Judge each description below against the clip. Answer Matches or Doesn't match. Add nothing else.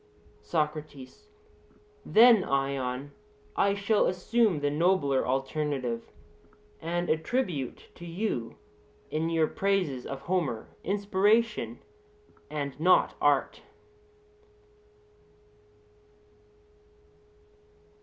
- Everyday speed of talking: Doesn't match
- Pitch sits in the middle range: Matches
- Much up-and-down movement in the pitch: Matches